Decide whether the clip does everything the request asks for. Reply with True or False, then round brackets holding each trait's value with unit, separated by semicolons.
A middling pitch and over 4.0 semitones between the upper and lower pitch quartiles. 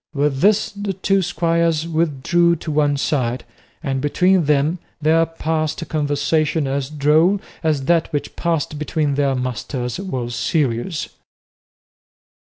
False (155 Hz; 3.1 semitones)